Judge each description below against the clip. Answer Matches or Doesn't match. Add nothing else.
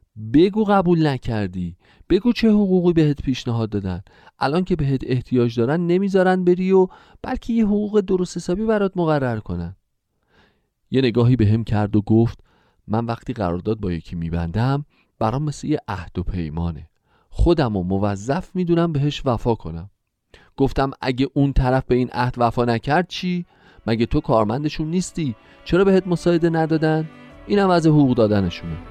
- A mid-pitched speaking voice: Doesn't match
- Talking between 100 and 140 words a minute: Doesn't match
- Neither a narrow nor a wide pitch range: Doesn't match